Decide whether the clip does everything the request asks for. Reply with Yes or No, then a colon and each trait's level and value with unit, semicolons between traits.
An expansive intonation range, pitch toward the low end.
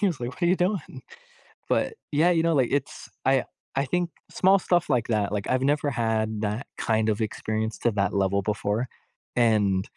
Yes: wide, 6.2 semitones; low, 120 Hz